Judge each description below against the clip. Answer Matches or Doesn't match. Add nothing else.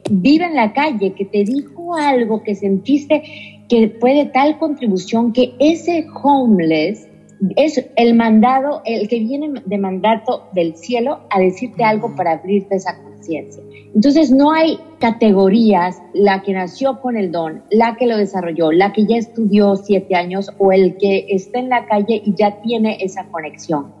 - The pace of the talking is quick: Doesn't match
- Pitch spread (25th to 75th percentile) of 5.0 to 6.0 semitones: Doesn't match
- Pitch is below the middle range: Doesn't match